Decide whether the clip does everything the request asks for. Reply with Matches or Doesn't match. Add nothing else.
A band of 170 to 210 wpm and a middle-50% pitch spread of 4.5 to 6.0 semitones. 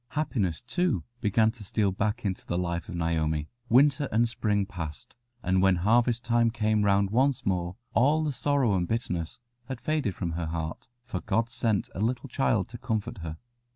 Matches